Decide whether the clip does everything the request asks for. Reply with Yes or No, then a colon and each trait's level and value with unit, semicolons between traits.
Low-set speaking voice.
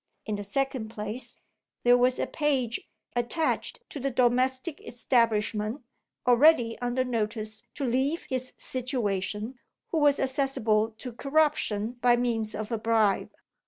No: high, 245 Hz